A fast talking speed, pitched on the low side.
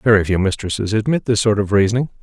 Yes: fast, 215 wpm; low, 105 Hz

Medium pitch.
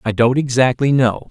No: low, 125 Hz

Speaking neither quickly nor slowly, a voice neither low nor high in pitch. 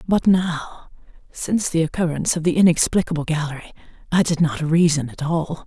Yes: average, 160 wpm; medium, 165 Hz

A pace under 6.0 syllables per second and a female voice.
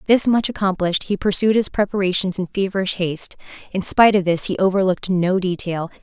No: 6.1 syllables/s; female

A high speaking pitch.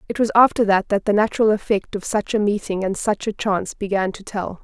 Yes: high, 205 Hz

